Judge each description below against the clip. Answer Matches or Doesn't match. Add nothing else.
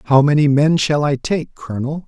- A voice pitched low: Doesn't match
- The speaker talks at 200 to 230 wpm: Matches